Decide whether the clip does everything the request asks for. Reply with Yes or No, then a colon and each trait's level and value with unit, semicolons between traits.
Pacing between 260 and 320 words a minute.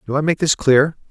Yes: fast, 270 wpm